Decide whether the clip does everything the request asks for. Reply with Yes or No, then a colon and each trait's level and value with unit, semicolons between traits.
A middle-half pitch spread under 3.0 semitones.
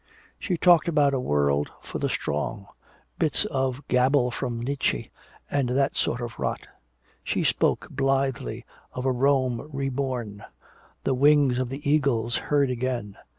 Yes: narrow, 2.6 semitones